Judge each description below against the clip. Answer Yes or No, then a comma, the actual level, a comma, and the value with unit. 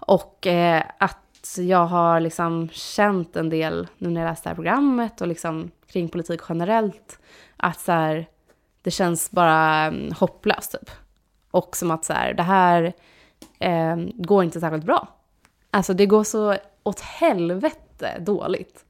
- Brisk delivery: No, average, 150 wpm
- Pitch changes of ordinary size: Yes, average, 3.0 semitones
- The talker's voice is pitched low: No, medium, 175 Hz